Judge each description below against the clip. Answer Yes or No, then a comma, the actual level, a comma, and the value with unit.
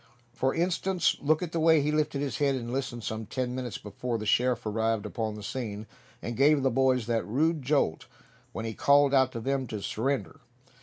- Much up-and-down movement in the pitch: No, average, 4.0 semitones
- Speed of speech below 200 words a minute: No, fast, 205 wpm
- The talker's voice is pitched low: Yes, low, 130 Hz